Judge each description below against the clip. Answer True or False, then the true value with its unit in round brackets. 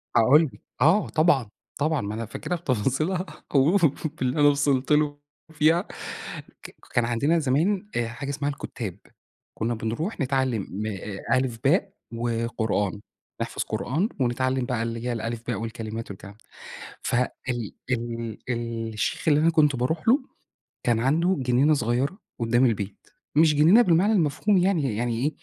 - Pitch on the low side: True (130 Hz)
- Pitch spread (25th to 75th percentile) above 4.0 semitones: True (5.0 semitones)